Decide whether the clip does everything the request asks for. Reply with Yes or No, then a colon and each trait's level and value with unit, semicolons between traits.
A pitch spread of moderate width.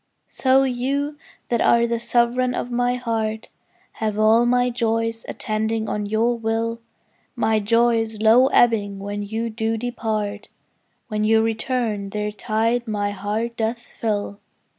No: narrow, 1.8 semitones